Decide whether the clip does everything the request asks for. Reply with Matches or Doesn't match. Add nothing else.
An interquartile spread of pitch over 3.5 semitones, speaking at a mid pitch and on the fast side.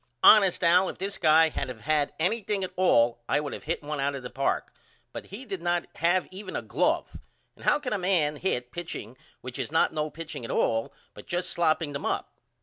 Matches